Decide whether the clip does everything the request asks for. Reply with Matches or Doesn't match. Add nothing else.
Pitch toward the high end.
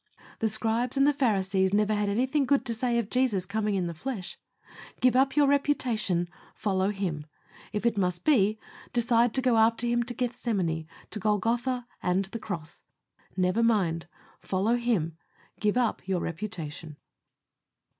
Matches